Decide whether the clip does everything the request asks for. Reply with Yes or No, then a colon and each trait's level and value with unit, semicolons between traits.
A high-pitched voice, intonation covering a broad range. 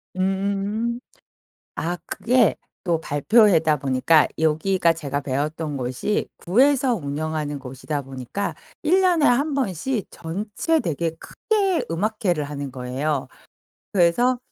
No: medium, 170 Hz; wide, 7.5 semitones